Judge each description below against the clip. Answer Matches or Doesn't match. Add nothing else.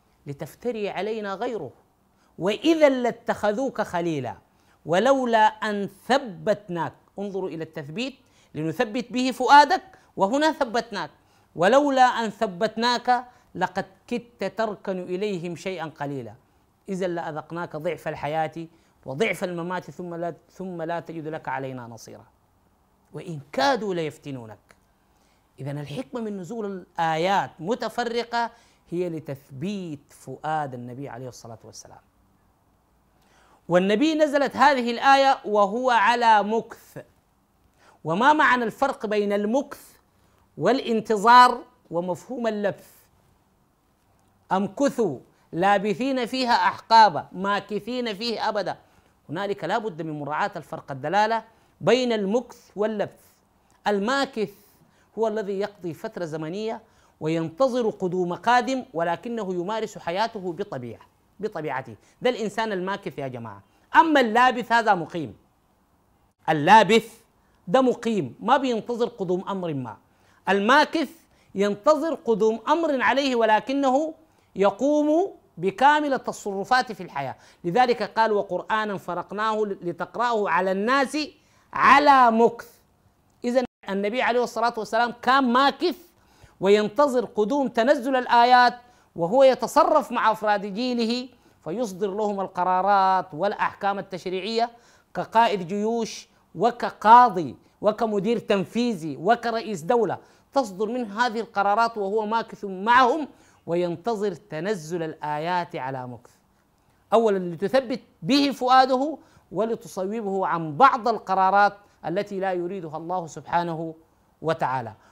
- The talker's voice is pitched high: Matches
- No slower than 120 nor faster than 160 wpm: Doesn't match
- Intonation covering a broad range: Matches